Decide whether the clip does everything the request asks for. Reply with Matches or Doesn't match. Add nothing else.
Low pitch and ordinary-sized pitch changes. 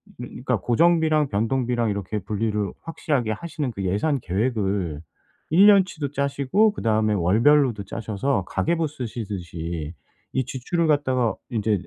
Doesn't match